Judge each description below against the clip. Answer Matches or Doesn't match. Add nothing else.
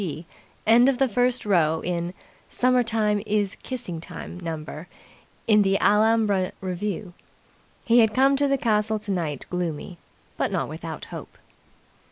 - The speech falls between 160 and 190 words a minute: Doesn't match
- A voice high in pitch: Matches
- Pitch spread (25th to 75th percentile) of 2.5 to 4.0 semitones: Doesn't match